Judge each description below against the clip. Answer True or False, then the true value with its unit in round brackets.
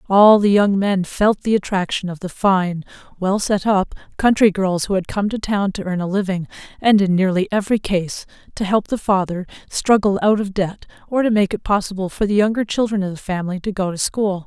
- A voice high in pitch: True (195 Hz)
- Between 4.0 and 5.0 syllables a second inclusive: False (5.4 syllables/s)